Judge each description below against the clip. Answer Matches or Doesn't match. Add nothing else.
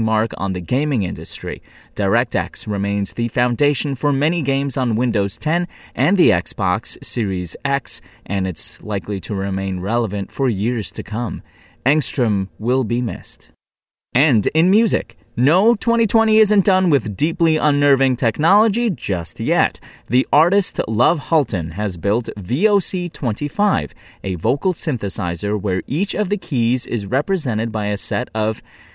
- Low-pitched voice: Matches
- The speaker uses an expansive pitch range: Matches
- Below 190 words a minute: Matches